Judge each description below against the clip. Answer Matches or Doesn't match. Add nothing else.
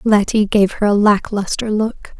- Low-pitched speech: Doesn't match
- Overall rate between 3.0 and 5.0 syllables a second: Matches